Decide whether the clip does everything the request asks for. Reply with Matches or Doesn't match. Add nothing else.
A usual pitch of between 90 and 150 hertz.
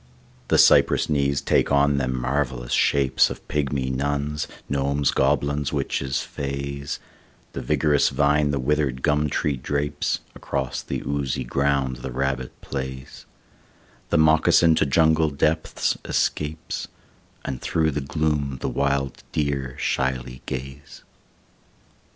Doesn't match